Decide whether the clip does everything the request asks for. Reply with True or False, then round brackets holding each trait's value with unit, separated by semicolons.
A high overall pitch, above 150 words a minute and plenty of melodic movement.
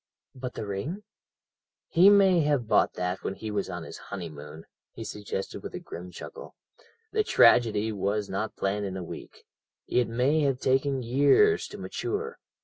False (115 Hz; 165 wpm; 7.0 semitones)